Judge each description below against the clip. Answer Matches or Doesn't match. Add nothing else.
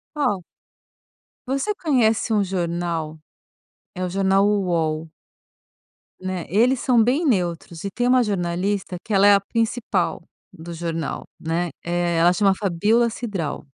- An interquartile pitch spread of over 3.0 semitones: Matches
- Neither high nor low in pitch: Doesn't match